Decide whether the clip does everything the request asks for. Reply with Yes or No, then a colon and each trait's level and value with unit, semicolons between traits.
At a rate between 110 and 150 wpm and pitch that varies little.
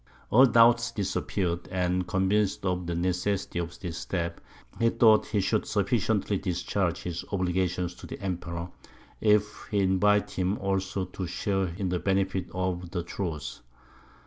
Yes: average, 145 wpm; narrow, 2.3 semitones